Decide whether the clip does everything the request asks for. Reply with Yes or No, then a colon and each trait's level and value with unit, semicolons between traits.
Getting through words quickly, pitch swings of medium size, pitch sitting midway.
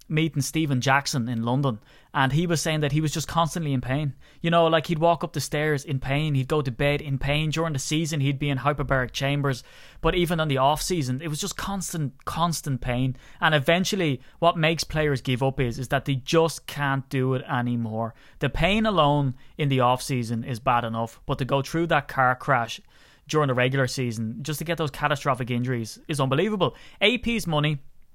Yes: fast, 210 wpm; average, 3.3 semitones; medium, 145 Hz